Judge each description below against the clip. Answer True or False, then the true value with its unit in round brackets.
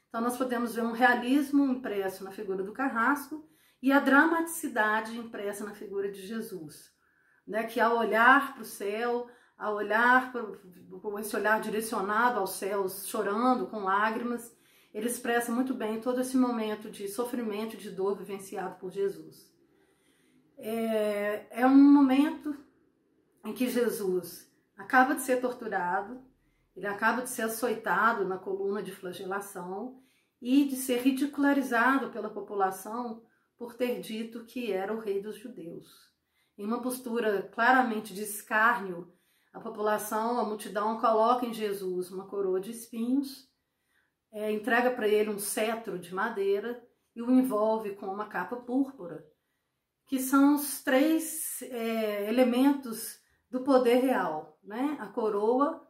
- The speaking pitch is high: True (225 Hz)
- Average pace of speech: True (140 wpm)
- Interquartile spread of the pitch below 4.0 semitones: True (3.6 semitones)